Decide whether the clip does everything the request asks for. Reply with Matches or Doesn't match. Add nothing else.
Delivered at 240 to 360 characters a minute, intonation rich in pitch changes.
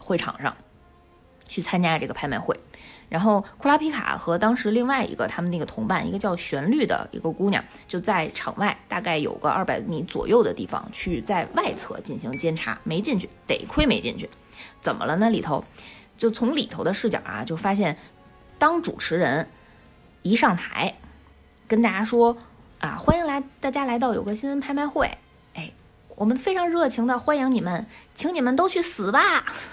Matches